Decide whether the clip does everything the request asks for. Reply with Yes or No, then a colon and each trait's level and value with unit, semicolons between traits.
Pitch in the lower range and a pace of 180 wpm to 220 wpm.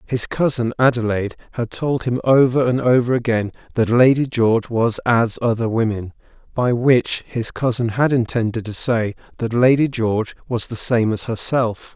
No: low, 120 Hz; average, 160 wpm